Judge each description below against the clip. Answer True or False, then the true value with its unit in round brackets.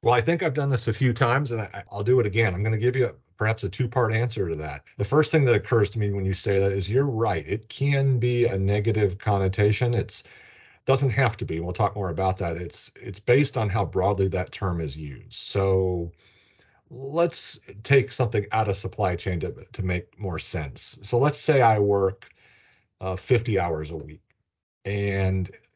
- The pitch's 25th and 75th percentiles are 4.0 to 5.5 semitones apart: True (4.3 semitones)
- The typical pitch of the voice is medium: False (105 Hz)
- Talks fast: True (215 wpm)